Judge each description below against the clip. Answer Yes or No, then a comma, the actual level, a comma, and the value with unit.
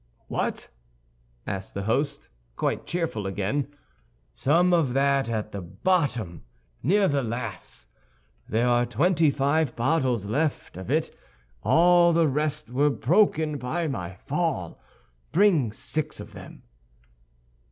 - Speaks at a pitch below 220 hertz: Yes, medium, 140 Hz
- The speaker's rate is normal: No, slow, 120 wpm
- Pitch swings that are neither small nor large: No, wide, 6.0 semitones